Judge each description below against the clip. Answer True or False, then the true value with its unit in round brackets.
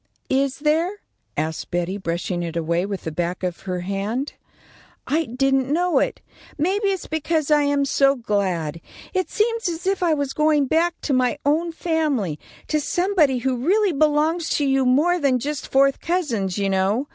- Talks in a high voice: True (275 Hz)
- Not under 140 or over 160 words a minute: False (175 wpm)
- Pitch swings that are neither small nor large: False (8.3 semitones)